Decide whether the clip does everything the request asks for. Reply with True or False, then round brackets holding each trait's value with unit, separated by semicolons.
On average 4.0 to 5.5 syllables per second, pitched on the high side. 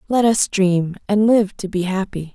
True (4.4 syllables/s; 200 Hz)